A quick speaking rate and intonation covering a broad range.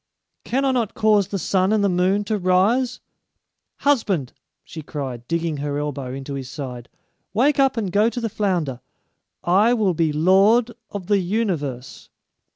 No: average, 160 wpm; wide, 6.7 semitones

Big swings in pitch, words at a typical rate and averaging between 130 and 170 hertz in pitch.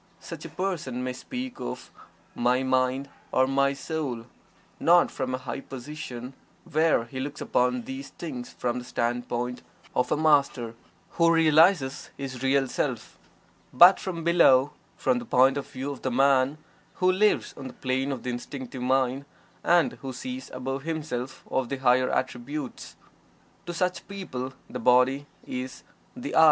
No: average, 3.7 semitones; average, 155 wpm; low, 135 Hz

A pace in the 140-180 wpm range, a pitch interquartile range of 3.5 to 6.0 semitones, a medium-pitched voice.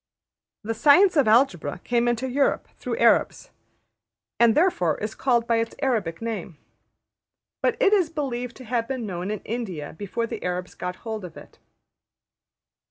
No: average, 160 wpm; average, 5.1 semitones; high, 230 Hz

